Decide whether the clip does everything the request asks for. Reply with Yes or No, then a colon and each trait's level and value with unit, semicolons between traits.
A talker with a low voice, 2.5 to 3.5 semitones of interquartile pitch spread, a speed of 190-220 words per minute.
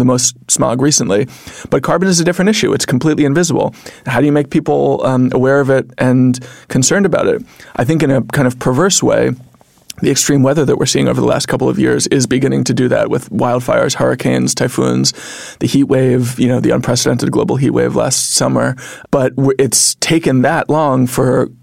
Yes: low, 130 Hz; average, 3.0 semitones; fast, 205 wpm